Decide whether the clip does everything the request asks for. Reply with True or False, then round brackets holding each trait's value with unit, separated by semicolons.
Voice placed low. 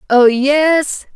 False (275 Hz)